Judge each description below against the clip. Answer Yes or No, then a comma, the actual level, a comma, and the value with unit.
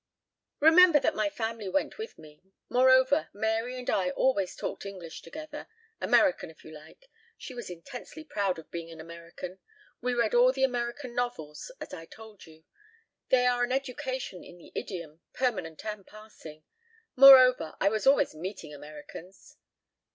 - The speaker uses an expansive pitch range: Yes, wide, 7.3 semitones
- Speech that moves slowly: No, average, 160 wpm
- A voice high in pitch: Yes, high, 220 Hz